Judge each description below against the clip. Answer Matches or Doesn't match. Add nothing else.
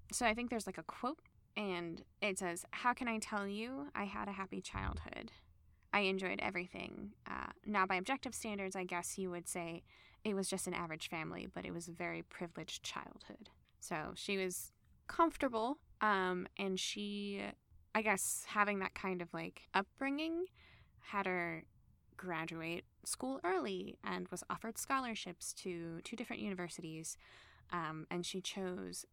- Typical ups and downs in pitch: Matches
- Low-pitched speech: Doesn't match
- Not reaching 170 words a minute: Matches